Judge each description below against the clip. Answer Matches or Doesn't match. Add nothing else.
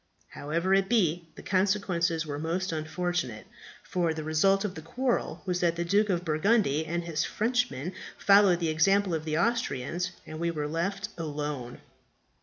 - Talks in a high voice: Doesn't match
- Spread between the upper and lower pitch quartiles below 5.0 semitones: Matches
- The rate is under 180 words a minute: Matches